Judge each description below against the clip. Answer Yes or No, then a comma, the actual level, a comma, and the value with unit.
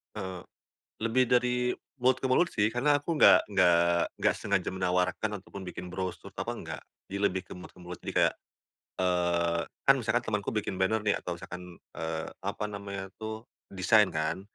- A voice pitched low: Yes, very low, 95 Hz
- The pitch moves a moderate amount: Yes, average, 3.7 semitones